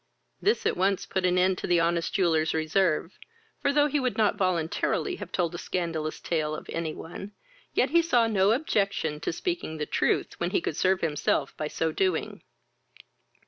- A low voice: No, medium, 180 Hz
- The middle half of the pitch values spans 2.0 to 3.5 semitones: No, average, 5.0 semitones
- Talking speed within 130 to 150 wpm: No, average, 185 wpm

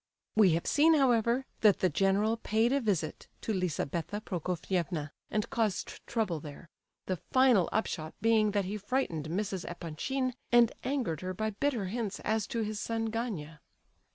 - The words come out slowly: No, average, 155 wpm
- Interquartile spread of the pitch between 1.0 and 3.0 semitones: No, average, 4.4 semitones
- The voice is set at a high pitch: Yes, high, 210 Hz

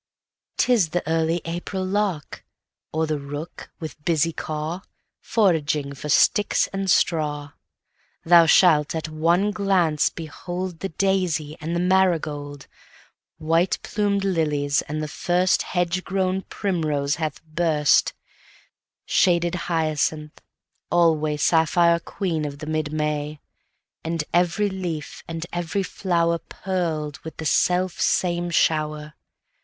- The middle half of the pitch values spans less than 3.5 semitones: Yes, average, 2.9 semitones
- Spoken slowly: Yes, slow, 100 wpm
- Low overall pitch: No, medium, 165 Hz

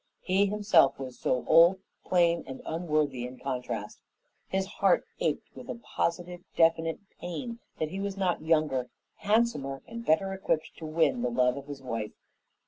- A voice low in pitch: No, medium, 165 Hz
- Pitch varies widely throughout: Yes, wide, 6.0 semitones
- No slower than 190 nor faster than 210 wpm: No, average, 160 wpm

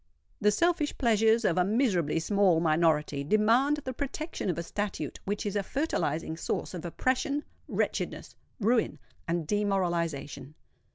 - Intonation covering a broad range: Yes, wide, 6.0 semitones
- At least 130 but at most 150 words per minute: Yes, slow, 135 wpm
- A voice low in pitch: No, high, 200 Hz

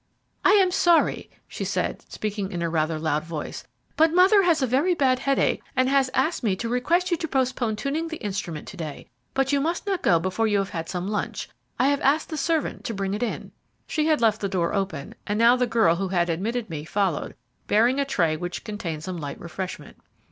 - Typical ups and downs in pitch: No, wide, 7.6 semitones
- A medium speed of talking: No, fast, 220 wpm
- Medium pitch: No, high, 220 Hz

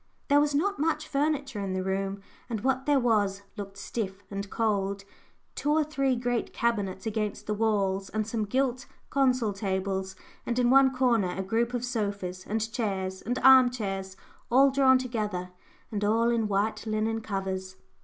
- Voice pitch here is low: No, high, 220 Hz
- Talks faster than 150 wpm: Yes, average, 170 wpm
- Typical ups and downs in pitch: Yes, average, 4.5 semitones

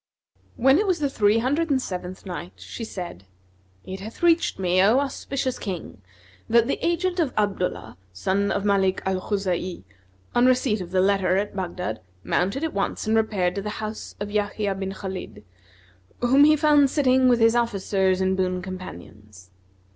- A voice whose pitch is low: No, high, 200 Hz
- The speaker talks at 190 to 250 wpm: No, average, 170 wpm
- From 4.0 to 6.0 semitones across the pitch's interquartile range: Yes, wide, 5.4 semitones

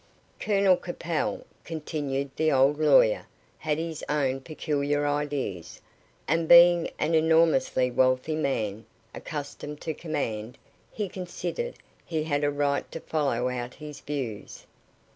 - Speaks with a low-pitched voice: No, medium, 150 Hz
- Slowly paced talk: Yes, slow, 125 wpm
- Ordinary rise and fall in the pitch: Yes, average, 3.3 semitones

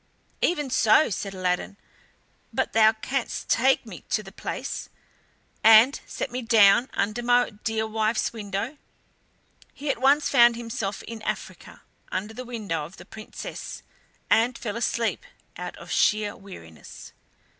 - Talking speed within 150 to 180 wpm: No, average, 140 wpm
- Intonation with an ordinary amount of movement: Yes, average, 3.1 semitones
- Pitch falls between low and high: No, high, 225 Hz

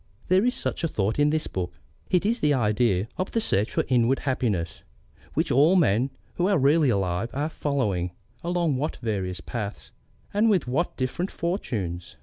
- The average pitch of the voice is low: Yes, low, 130 Hz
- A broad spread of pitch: Yes, wide, 8.6 semitones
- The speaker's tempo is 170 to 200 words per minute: Yes, average, 175 wpm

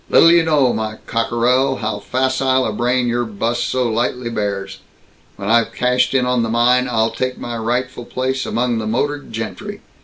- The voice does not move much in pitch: Yes, narrow, 2.2 semitones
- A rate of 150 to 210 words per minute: Yes, average, 180 wpm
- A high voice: No, low, 120 Hz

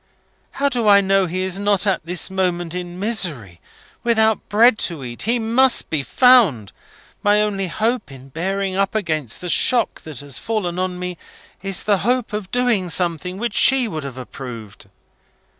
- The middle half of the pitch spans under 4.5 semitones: No, average, 4.9 semitones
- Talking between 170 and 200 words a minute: Yes, average, 175 wpm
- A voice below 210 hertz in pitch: Yes, high, 190 Hz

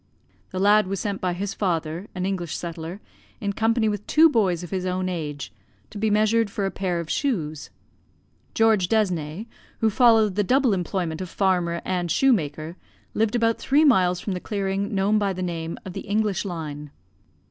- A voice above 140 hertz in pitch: Yes, high, 190 Hz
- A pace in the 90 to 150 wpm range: No, average, 180 wpm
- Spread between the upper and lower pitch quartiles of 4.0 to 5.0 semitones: No, average, 3.6 semitones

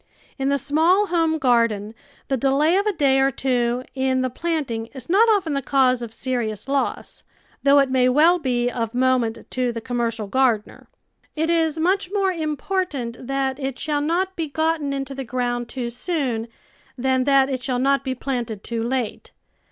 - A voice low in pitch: No, very high, 265 Hz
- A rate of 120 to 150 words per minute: No, average, 185 wpm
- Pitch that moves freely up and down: No, average, 4.1 semitones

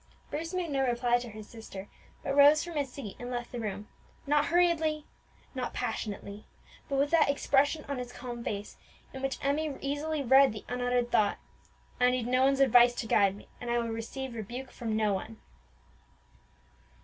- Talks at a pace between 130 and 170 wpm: No, average, 185 wpm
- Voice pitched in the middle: No, very high, 250 Hz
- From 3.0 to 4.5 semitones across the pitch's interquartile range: Yes, average, 3.6 semitones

